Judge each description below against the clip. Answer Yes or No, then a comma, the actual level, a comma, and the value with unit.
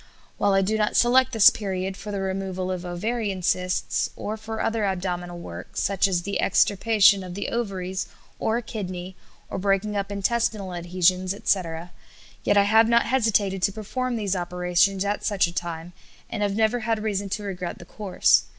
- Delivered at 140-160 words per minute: No, average, 180 wpm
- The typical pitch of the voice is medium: No, high, 195 Hz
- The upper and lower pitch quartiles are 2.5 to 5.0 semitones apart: Yes, average, 2.8 semitones